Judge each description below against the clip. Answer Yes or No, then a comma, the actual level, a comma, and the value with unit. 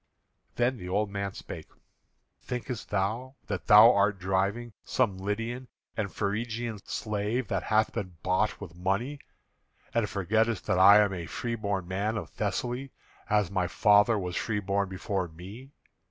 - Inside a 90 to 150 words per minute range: Yes, average, 145 wpm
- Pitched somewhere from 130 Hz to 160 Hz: No, low, 105 Hz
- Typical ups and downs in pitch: Yes, average, 3.0 semitones